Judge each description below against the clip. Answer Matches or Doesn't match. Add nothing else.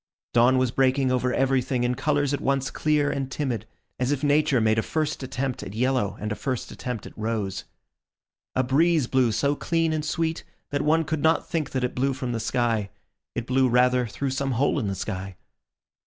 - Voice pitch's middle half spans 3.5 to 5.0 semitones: Doesn't match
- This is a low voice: Matches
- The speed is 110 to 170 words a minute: Doesn't match